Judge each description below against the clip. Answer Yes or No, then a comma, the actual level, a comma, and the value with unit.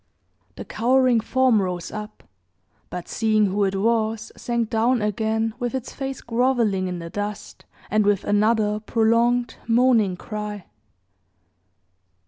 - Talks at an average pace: No, slow, 125 wpm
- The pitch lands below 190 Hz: No, high, 220 Hz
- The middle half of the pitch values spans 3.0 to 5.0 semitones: No, narrow, 2.4 semitones